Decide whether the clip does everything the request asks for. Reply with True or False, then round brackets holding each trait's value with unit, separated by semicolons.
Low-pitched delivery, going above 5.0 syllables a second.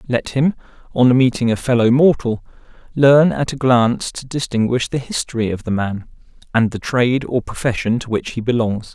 True (120 Hz; 5.2 syllables/s)